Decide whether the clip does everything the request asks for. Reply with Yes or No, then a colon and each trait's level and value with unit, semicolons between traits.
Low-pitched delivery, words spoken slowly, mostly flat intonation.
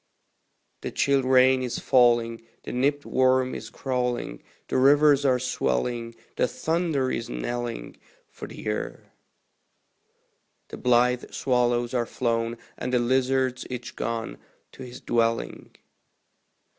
Yes: low, 125 Hz; slow, 120 wpm; narrow, 1.8 semitones